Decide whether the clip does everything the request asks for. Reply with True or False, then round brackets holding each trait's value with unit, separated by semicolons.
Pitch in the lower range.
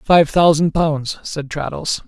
False (155 Hz)